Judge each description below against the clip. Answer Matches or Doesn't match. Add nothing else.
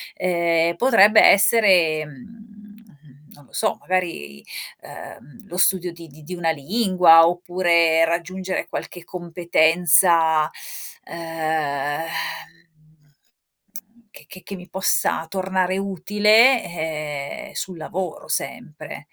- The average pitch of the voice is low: Doesn't match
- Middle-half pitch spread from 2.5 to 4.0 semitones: Matches